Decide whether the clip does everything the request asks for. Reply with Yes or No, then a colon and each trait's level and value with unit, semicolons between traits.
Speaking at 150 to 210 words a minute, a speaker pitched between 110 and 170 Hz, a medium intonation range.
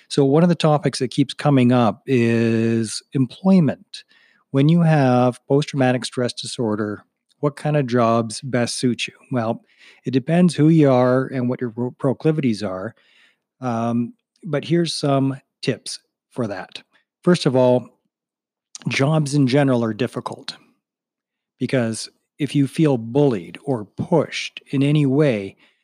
No: average, 140 wpm; low, 135 Hz; average, 3.4 semitones